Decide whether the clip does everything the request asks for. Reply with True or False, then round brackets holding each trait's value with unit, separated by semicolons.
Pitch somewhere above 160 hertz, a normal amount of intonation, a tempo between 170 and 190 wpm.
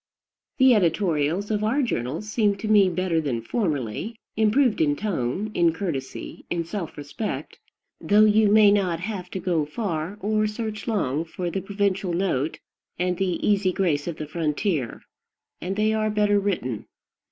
False (190 Hz; 4.7 semitones; 160 wpm)